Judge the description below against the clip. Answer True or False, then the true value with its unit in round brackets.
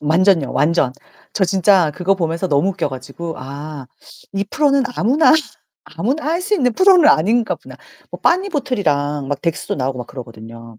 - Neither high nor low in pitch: True (170 Hz)